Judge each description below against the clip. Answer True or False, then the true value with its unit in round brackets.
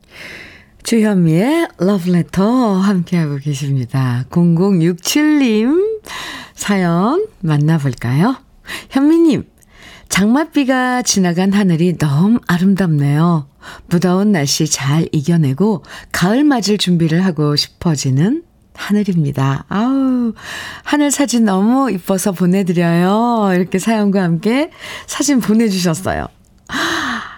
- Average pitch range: False (5.7 semitones)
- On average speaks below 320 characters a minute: True (230 characters per minute)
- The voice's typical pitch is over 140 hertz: True (190 Hz)